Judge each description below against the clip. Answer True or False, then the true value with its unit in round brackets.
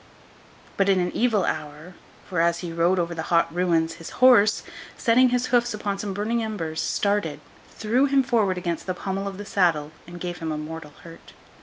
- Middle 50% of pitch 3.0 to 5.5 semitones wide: True (4.1 semitones)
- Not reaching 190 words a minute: False (195 wpm)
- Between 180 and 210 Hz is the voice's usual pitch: True (185 Hz)